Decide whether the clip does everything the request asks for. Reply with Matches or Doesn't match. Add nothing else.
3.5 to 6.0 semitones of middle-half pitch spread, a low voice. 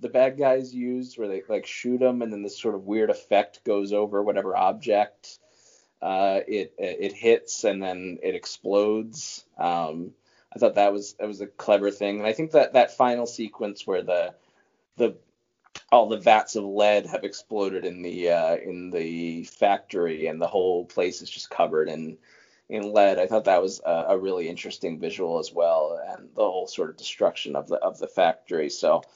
Matches